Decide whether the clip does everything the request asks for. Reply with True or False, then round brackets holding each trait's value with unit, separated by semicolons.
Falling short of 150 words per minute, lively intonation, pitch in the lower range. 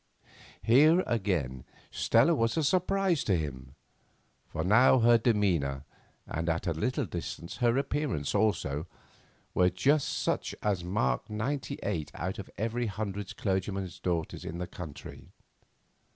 True (135 wpm; 6.2 semitones; 100 Hz)